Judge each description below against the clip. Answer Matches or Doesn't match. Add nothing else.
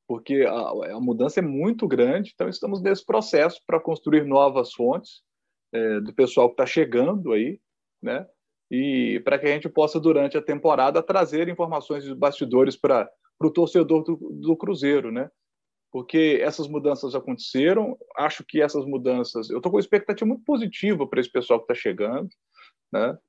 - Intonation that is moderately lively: Doesn't match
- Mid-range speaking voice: Matches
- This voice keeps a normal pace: Matches